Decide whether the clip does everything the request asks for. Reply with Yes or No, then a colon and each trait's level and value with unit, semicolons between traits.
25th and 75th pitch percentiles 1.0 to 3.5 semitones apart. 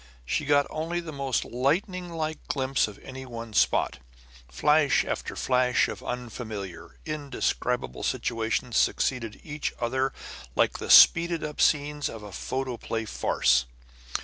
No: average, 4.6 semitones